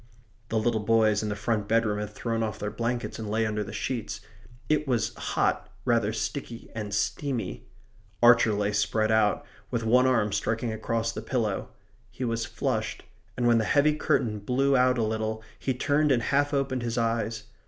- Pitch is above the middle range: No, low, 115 Hz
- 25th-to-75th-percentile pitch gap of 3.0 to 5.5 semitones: No, narrow, 2.5 semitones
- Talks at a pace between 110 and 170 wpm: No, average, 185 wpm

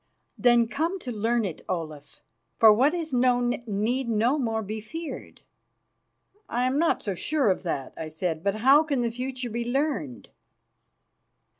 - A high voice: Yes, high, 235 Hz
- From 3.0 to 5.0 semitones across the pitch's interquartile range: Yes, average, 4.7 semitones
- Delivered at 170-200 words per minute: No, average, 160 wpm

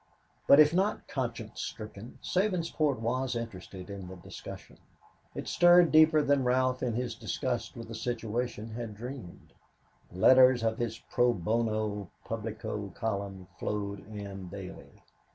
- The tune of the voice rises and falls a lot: No, average, 3.7 semitones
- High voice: No, low, 115 Hz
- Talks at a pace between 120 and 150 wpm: Yes, slow, 135 wpm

